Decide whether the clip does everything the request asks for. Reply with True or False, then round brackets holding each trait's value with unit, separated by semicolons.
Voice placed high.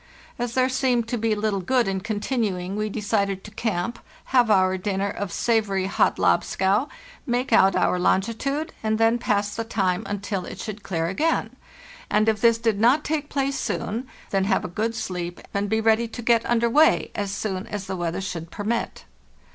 True (215 Hz)